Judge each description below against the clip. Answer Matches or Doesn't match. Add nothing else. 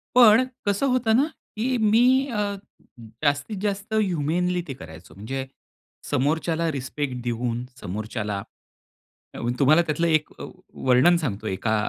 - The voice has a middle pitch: Matches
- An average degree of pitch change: Doesn't match